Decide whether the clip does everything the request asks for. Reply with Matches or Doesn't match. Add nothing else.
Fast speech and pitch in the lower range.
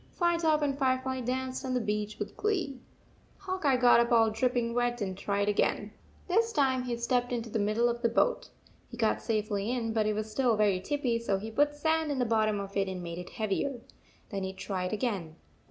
Doesn't match